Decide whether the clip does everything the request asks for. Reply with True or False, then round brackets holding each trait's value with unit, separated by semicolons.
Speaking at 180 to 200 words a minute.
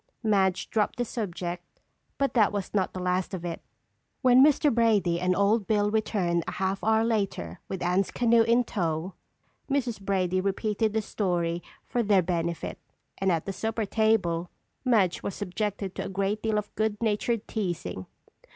False (165 wpm)